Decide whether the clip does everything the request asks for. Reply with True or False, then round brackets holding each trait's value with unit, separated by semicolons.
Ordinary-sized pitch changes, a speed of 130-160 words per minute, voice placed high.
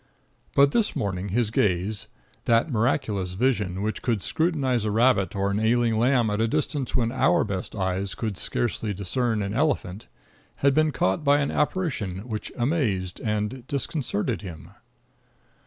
False (4.8 semitones; 155 wpm; 110 Hz)